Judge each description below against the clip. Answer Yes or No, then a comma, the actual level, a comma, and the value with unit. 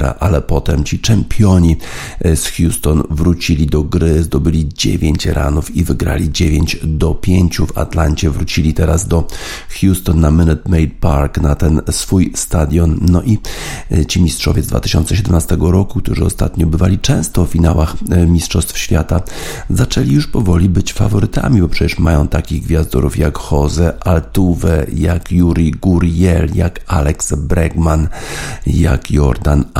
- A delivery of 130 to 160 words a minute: Yes, average, 135 wpm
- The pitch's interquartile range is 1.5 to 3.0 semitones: Yes, narrow, 2.4 semitones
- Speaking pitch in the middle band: No, very low, 85 Hz